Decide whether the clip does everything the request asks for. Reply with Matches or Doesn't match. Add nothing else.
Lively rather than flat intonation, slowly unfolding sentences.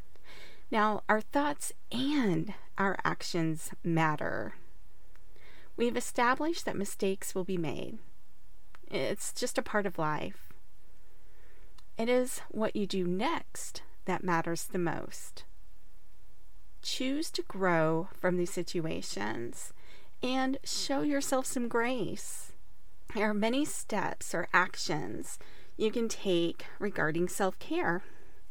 Matches